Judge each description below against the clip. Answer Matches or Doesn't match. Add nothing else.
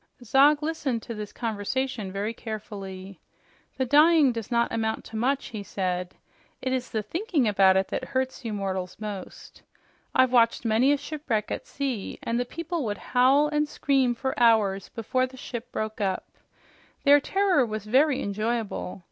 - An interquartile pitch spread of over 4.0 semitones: Matches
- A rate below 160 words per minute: Doesn't match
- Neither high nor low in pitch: Doesn't match